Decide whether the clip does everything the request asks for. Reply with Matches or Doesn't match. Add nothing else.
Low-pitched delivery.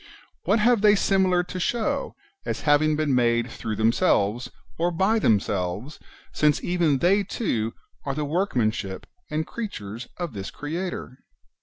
Doesn't match